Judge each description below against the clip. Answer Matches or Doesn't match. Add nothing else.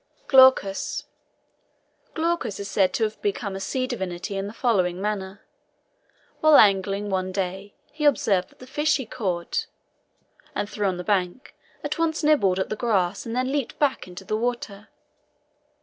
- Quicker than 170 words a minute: Doesn't match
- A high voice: Matches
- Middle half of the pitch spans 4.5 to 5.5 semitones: Matches